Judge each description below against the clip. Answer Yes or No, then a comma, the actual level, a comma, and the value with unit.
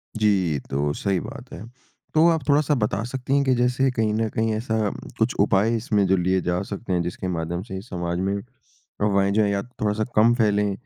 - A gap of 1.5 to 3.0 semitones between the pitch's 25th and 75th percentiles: No, average, 3.6 semitones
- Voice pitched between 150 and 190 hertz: No, low, 105 Hz